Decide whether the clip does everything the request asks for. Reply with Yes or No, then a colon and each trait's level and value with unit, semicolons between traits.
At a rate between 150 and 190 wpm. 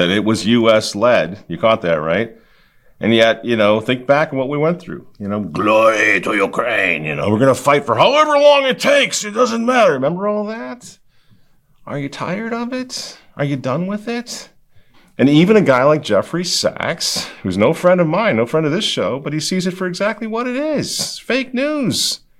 No: fast, 205 wpm